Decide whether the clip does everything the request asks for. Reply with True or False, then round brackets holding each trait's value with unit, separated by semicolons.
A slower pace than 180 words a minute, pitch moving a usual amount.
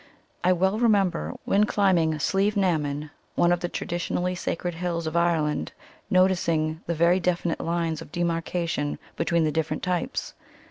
False (150 wpm; 2.1 semitones)